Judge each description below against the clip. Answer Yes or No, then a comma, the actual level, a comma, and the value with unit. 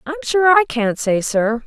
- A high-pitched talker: Yes, very high, 280 Hz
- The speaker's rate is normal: No, fast, 215 wpm